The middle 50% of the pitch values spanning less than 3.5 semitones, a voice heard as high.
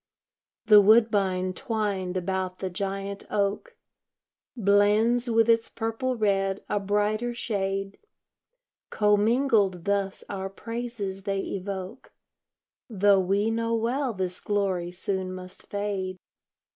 Yes: average, 2.7 semitones; high, 200 Hz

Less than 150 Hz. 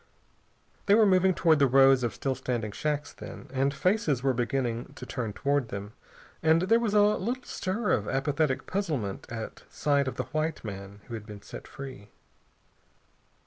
Yes: low, 135 Hz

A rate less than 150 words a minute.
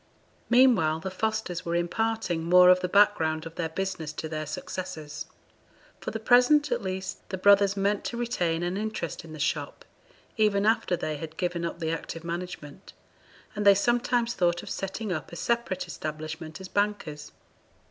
No: average, 170 wpm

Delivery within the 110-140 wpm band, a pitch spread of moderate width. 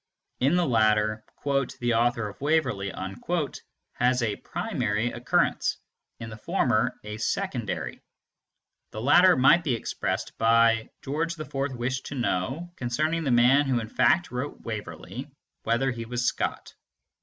Yes: slow, 135 wpm; average, 3.8 semitones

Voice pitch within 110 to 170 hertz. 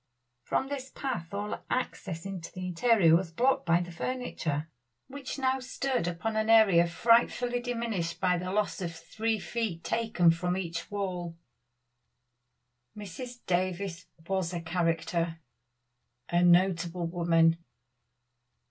No: medium, 185 Hz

